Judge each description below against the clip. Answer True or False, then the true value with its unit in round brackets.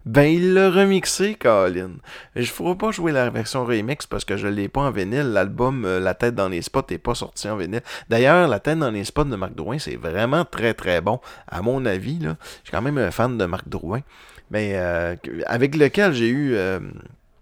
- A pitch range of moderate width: False (7.5 semitones)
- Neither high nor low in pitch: False (120 Hz)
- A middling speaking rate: False (225 wpm)